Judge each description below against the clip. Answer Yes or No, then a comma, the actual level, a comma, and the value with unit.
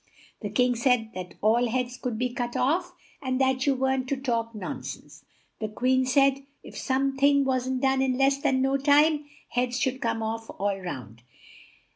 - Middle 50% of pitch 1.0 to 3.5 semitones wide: Yes, average, 2.8 semitones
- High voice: Yes, very high, 255 Hz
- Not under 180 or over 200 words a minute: Yes, average, 185 wpm